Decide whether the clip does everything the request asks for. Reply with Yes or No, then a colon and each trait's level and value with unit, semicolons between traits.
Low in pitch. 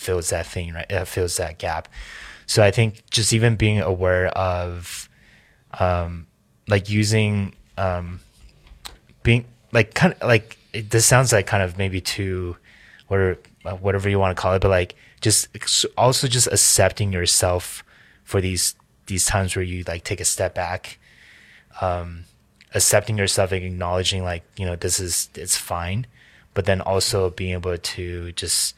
Yes: very low, 95 Hz